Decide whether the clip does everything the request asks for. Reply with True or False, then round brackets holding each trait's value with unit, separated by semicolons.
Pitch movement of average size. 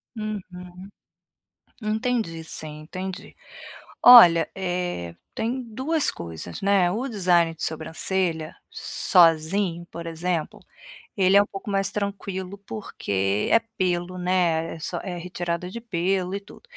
True (3.3 semitones)